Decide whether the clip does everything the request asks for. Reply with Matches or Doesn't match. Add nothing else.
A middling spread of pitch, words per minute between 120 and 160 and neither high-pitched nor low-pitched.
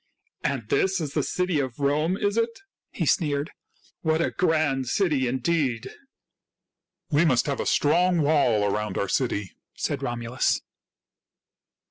Matches